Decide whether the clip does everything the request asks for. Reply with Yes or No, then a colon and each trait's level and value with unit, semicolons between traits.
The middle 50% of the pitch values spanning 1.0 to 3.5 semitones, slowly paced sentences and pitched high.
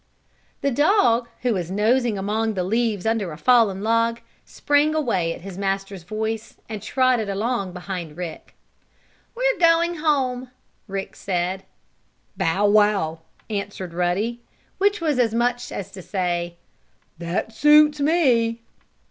No: average, 4.7 semitones; slow, 130 wpm; high, 220 Hz